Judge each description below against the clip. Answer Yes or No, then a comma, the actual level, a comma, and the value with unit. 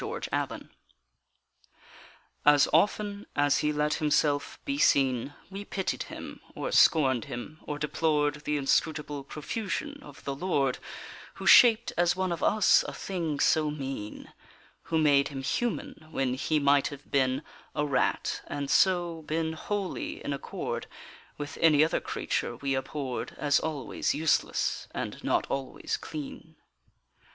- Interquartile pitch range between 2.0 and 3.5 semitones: Yes, average, 3.1 semitones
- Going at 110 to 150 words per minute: Yes, average, 140 wpm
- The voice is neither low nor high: Yes, medium, 150 Hz